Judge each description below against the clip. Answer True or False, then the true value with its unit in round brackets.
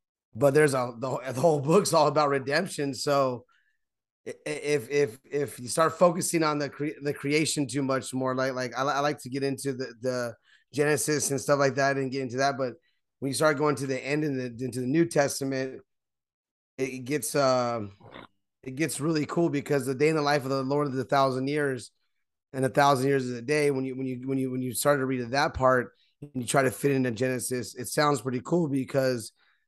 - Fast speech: True (220 wpm)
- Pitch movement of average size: False (2.2 semitones)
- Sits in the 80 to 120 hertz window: False (135 Hz)